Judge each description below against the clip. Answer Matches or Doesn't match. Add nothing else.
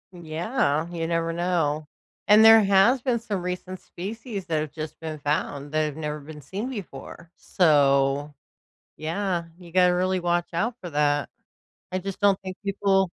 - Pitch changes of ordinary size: Matches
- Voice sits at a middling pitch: Matches